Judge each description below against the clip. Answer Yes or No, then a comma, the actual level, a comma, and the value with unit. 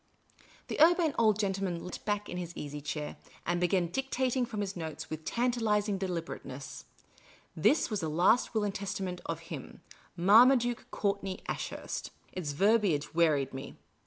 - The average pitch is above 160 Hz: Yes, high, 190 Hz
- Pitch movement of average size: Yes, average, 4.8 semitones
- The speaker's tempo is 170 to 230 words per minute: No, average, 155 wpm